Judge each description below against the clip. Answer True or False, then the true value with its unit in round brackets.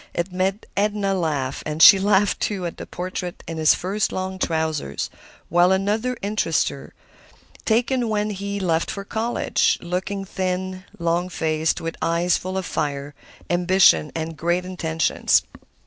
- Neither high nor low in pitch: True (180 Hz)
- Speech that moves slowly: False (145 wpm)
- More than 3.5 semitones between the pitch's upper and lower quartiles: False (3.2 semitones)